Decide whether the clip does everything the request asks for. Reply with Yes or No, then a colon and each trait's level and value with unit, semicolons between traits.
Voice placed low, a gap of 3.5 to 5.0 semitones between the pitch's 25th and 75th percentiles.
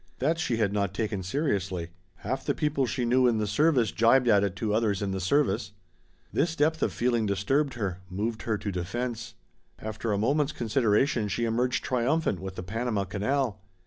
Yes: low, 115 Hz; average, 4.4 semitones